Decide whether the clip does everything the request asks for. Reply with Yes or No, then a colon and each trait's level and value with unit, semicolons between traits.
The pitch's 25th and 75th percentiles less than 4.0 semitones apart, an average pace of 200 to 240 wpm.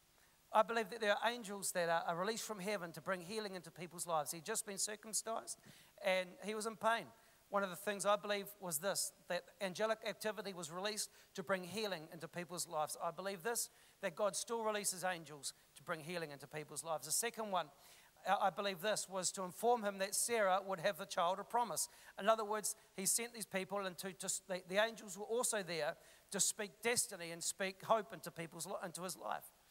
Yes: average, 3.1 semitones; fast, 205 wpm